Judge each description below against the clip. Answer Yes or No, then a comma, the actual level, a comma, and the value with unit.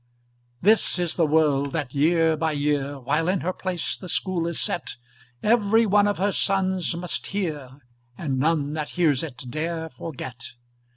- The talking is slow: No, average, 165 wpm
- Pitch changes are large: No, average, 4.2 semitones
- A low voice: No, medium, 160 Hz